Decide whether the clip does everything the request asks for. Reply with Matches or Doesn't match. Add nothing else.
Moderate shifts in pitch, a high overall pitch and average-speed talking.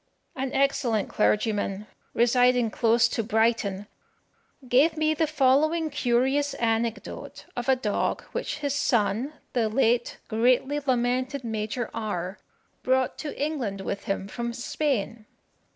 Doesn't match